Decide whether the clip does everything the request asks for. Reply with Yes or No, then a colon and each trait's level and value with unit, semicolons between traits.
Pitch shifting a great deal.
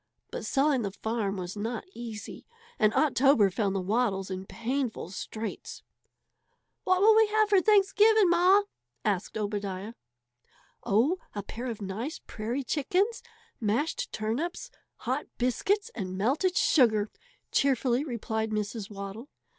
Yes: wide, 7.3 semitones